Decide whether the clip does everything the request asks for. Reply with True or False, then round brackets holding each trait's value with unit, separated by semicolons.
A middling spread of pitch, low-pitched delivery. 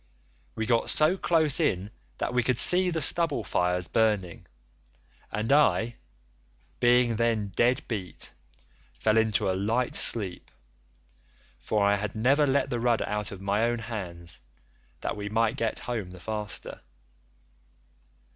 True (3.3 semitones; 110 Hz)